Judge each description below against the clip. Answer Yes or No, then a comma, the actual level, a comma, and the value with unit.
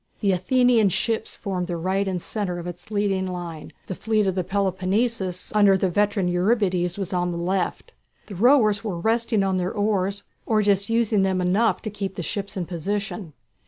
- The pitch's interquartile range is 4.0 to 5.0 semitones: No, narrow, 2.6 semitones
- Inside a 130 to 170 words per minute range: No, average, 190 wpm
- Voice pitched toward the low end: No, high, 195 Hz